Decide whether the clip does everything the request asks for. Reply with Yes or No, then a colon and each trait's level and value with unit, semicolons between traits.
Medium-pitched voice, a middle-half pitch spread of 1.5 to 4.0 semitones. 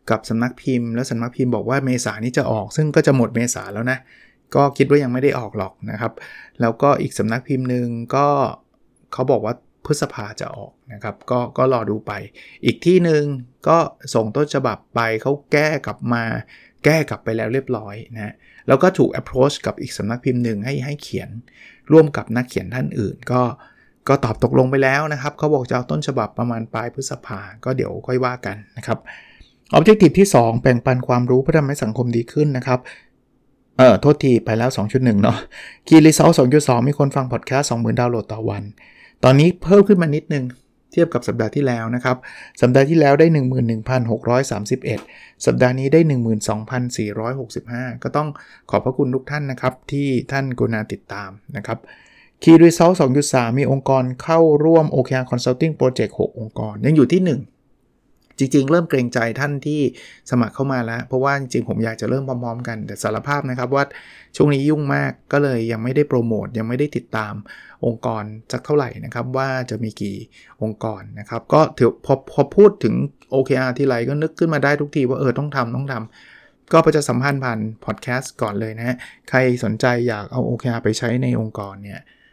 No: low, 125 Hz; average, 3.6 semitones